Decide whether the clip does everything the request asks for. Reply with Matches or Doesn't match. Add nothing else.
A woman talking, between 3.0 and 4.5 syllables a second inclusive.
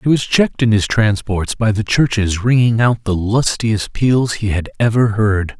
Doesn't match